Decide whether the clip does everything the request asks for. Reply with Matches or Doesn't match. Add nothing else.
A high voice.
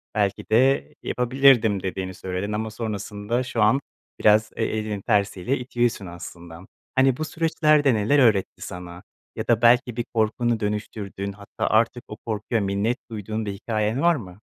Doesn't match